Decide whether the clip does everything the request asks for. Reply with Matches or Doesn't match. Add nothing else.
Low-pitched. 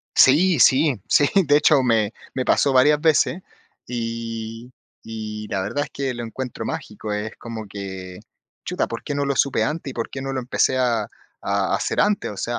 Matches